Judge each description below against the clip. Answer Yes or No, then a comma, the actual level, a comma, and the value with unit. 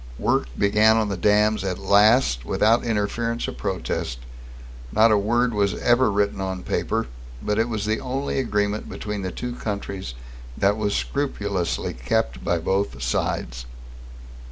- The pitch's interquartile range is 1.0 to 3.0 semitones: Yes, narrow, 2.6 semitones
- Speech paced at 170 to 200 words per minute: No, average, 150 wpm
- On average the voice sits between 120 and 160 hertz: No, low, 105 Hz